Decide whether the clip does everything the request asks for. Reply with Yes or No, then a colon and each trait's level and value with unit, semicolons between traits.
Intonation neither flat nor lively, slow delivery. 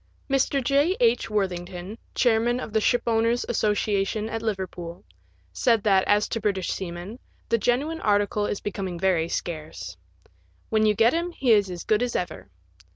No: average, 4.1 semitones; average, 175 wpm